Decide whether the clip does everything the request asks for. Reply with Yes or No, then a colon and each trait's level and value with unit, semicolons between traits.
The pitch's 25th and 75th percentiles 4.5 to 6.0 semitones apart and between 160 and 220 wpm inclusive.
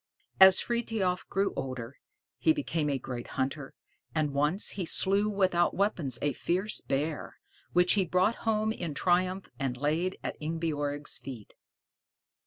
No: average, 5.1 semitones; average, 140 wpm